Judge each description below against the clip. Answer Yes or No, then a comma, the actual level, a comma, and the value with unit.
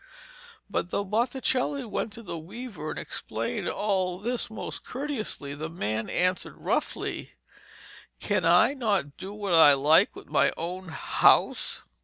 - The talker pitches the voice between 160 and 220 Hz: Yes, high, 190 Hz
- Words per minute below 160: Yes, average, 140 wpm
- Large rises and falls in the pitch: Yes, wide, 5.7 semitones